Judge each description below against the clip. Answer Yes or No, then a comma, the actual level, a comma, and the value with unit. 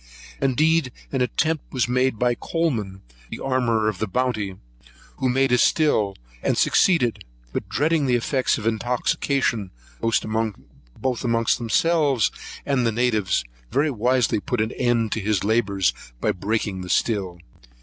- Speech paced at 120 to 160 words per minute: Yes, average, 140 wpm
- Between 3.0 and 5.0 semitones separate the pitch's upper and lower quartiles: Yes, average, 3.5 semitones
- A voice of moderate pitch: No, low, 120 Hz